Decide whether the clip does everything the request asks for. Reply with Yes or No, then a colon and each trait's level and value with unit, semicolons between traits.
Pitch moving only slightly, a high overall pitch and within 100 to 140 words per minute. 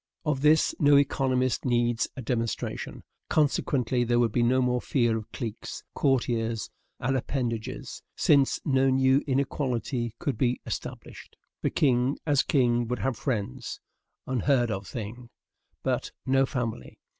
No: narrow, 2.2 semitones; low, 125 Hz; slow, 135 wpm